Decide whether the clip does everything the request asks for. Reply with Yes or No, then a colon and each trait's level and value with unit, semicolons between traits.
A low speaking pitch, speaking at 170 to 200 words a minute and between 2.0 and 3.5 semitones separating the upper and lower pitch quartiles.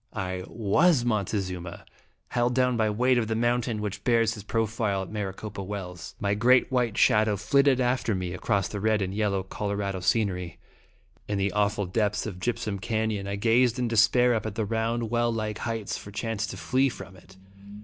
Yes: low, 110 Hz; average, 195 wpm; average, 3.0 semitones